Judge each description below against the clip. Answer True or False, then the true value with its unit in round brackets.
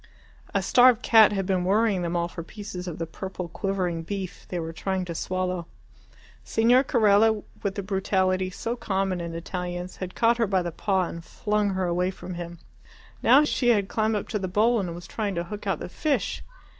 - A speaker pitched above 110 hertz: True (190 Hz)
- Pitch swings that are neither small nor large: True (3.0 semitones)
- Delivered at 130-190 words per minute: False (205 wpm)